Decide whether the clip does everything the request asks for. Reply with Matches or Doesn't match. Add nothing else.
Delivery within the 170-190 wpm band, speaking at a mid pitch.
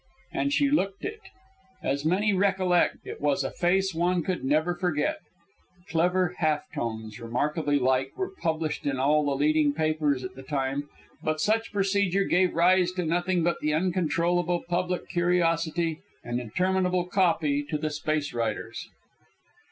Doesn't match